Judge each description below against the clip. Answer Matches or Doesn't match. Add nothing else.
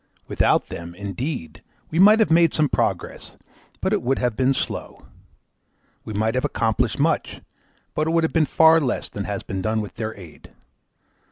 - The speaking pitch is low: Matches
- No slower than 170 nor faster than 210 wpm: Matches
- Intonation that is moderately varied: Doesn't match